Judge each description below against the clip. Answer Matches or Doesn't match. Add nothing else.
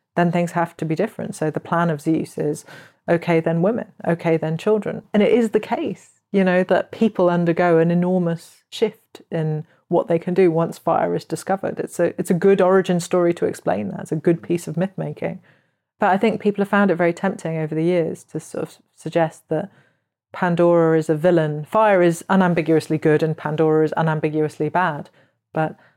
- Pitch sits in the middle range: Matches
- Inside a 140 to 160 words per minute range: Doesn't match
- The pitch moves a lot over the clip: Doesn't match